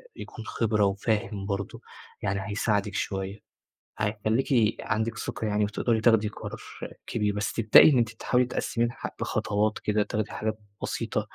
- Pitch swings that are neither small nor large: No, narrow, 1.7 semitones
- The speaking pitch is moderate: No, low, 105 Hz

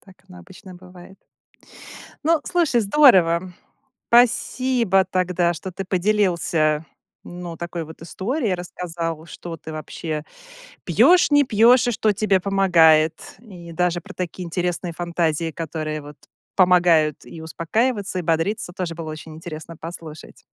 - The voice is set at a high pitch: No, medium, 175 Hz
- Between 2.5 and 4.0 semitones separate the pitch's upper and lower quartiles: Yes, average, 3.3 semitones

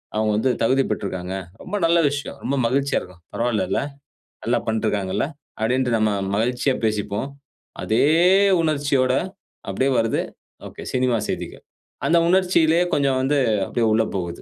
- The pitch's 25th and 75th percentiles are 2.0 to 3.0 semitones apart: No, average, 4.3 semitones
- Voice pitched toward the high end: No, low, 125 Hz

